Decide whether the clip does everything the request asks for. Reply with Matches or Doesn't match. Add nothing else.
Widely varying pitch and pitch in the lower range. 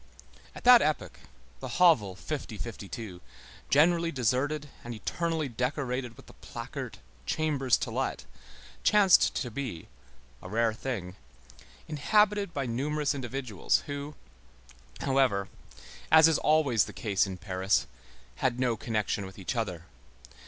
Matches